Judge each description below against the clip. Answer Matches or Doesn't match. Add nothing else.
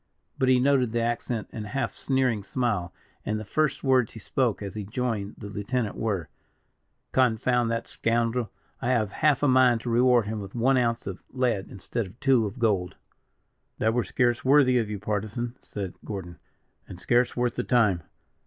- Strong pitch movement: Doesn't match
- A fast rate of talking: Doesn't match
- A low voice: Matches